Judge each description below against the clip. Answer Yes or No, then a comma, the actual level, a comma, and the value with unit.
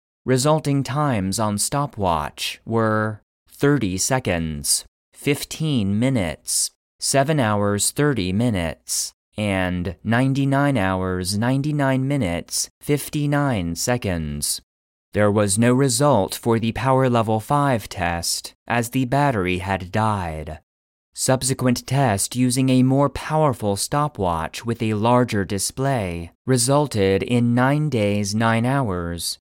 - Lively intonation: Yes, wide, 6.0 semitones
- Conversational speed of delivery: No, slow, 105 wpm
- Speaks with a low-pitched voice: Yes, low, 115 Hz